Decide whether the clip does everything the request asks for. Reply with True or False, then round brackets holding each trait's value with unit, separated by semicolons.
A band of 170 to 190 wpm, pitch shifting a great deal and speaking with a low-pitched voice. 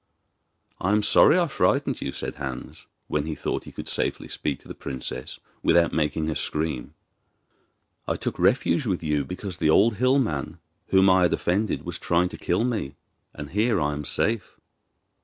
True (180 wpm; 6.1 semitones; 85 Hz)